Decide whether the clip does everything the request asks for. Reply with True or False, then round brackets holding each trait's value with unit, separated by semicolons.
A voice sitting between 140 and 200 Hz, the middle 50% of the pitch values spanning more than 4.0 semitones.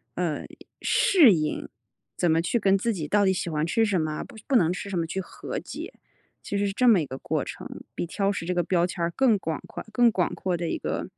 False (185 Hz; 3.6 semitones)